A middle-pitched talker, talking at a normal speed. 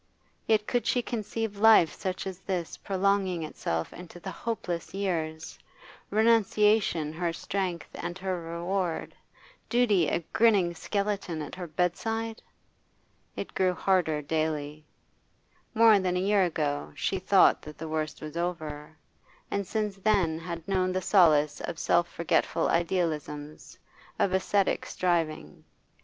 No: medium, 180 Hz; slow, 130 wpm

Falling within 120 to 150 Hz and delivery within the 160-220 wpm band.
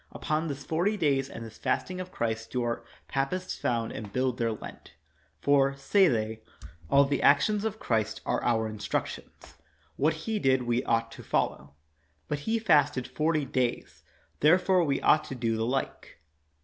Yes: low, 135 Hz; average, 170 wpm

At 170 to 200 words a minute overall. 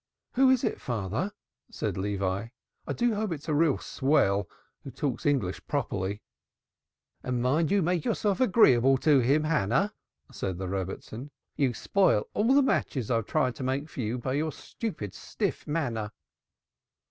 No: average, 160 wpm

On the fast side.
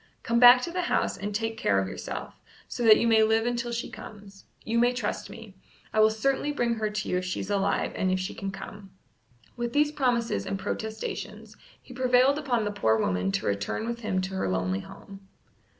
Yes: fast, 215 wpm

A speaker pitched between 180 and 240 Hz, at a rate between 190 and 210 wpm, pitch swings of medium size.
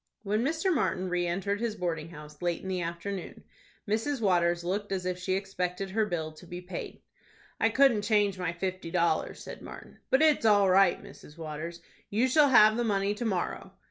Yes: high, 190 Hz; average, 195 wpm; average, 3.5 semitones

